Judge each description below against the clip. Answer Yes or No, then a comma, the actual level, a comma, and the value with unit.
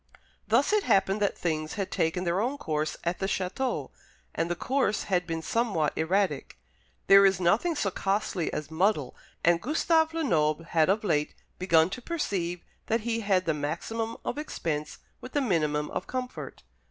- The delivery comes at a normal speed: Yes, average, 170 wpm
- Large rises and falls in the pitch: Yes, wide, 5.7 semitones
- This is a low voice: No, high, 190 Hz